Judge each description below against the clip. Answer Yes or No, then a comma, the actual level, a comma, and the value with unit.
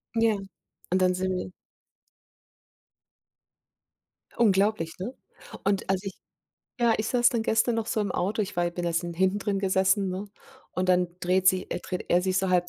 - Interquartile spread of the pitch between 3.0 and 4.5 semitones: No, narrow, 2.4 semitones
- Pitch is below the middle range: No, high, 190 Hz